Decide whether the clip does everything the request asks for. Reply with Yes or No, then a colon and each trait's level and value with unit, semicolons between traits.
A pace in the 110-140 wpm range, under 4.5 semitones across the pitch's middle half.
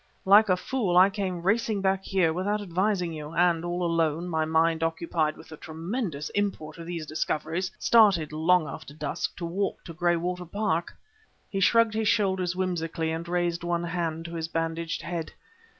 No: average, 175 wpm; narrow, 2.6 semitones